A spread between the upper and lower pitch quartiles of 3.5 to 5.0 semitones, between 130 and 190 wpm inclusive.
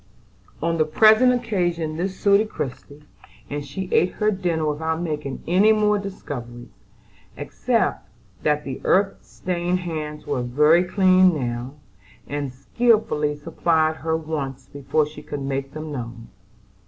Yes: average, 4.3 semitones; slow, 135 wpm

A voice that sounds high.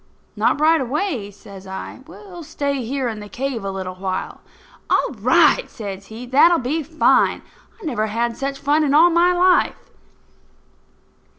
Yes: very high, 270 Hz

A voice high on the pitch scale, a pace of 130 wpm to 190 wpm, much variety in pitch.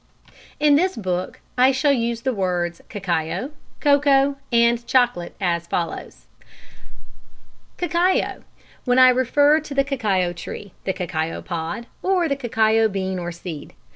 Yes: high, 235 Hz; average, 140 wpm; wide, 7.4 semitones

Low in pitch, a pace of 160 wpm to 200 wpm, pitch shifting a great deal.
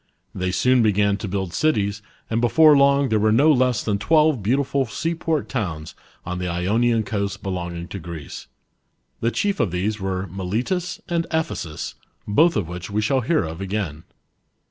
Yes: low, 105 Hz; average, 165 wpm; wide, 6.7 semitones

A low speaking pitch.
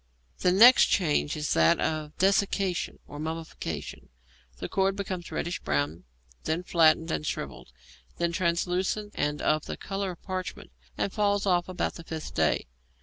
No: medium, 175 Hz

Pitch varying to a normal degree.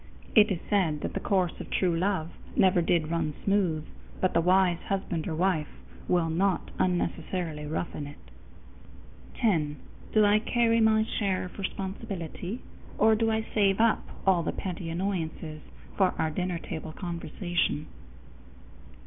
Yes: average, 3.4 semitones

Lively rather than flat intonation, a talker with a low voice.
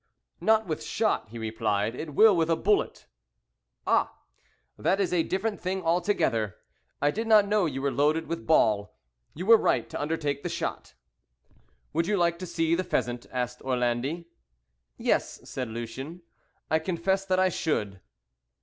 No: wide, 6.9 semitones; medium, 165 Hz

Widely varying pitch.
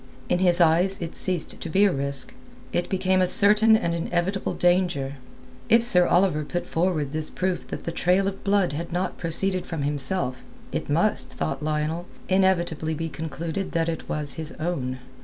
No: average, 3.3 semitones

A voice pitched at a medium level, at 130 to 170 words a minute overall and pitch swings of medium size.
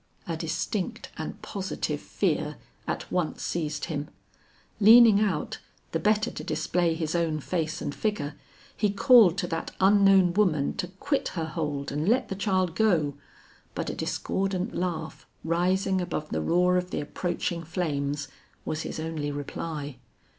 Yes: medium, 175 Hz; average, 150 wpm; average, 3.9 semitones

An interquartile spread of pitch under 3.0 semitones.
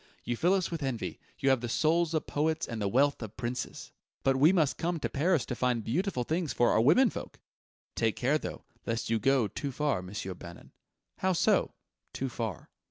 No: wide, 5.5 semitones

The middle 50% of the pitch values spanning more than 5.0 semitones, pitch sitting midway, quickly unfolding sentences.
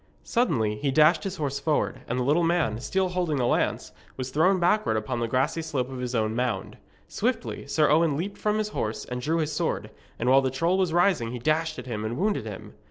Yes: wide, 5.6 semitones; medium, 145 Hz; fast, 230 wpm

